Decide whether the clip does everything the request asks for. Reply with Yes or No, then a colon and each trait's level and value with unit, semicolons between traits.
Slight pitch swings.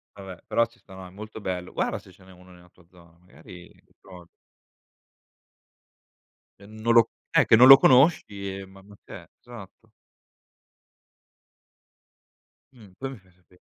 No: average, 3.4 semitones